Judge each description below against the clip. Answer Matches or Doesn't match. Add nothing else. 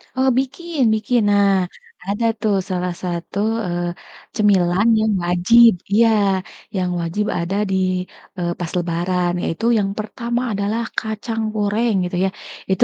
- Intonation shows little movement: Doesn't match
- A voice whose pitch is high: Matches